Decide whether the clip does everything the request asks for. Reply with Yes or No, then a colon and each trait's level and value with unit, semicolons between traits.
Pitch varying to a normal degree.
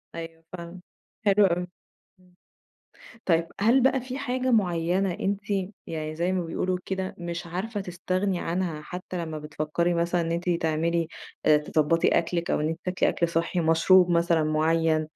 No: narrow, 2.1 semitones